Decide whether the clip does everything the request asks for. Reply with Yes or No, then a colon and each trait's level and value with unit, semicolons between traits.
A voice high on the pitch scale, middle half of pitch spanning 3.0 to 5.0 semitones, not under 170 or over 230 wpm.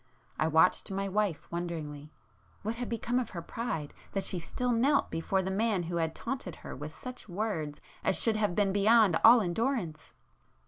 No: high, 195 Hz; wide, 5.6 semitones; average, 175 wpm